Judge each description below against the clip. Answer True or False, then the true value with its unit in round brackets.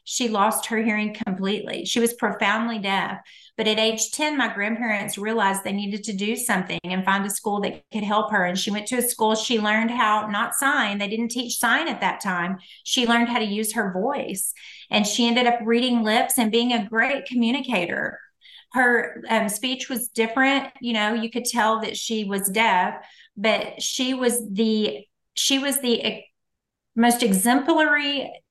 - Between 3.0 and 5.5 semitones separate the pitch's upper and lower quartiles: False (2.5 semitones)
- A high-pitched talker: True (225 Hz)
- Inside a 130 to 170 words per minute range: False (185 wpm)